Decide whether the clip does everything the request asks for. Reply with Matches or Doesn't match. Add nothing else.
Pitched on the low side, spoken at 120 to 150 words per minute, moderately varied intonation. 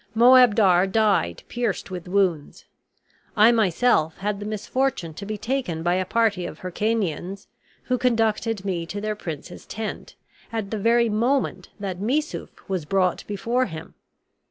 Doesn't match